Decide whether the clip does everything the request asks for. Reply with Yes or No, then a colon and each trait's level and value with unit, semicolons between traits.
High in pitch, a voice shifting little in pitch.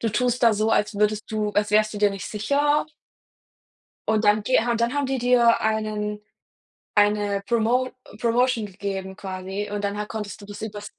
Yes: high, 215 Hz; narrow, 2.1 semitones